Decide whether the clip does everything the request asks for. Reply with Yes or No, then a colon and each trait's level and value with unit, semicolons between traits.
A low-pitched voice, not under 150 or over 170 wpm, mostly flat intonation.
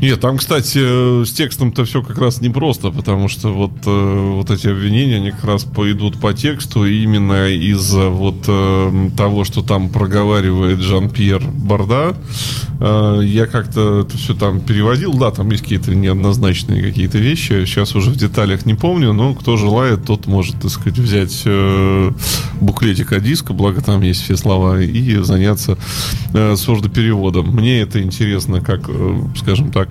No: low, 105 Hz; average, 155 wpm; average, 3.7 semitones